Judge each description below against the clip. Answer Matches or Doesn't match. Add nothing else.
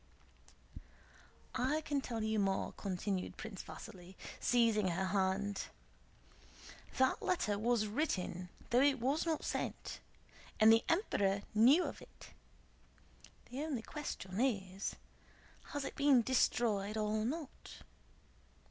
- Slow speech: Matches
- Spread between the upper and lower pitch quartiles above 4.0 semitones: Matches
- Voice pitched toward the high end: Matches